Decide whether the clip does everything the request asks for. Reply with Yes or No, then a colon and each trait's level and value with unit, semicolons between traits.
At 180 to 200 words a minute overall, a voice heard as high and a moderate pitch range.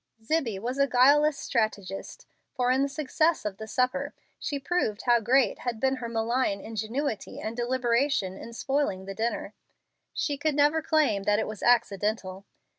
No: average, 165 wpm; high, 245 Hz; average, 4.4 semitones